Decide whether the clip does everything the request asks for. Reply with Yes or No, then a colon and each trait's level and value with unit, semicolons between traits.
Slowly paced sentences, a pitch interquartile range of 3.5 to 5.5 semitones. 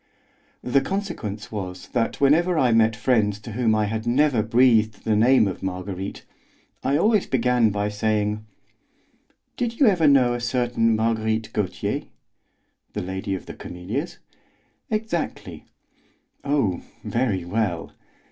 Yes: slow, 130 wpm; average, 4.2 semitones